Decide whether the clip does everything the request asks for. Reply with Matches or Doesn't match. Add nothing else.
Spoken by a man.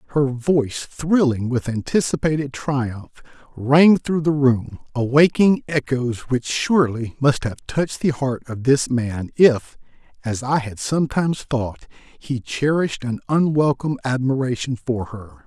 Matches